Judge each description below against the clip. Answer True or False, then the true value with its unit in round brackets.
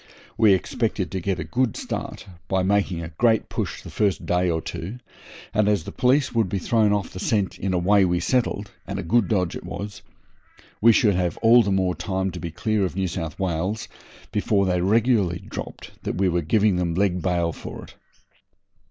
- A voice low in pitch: True (95 Hz)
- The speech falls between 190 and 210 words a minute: True (205 wpm)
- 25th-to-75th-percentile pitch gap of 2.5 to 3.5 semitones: True (3.0 semitones)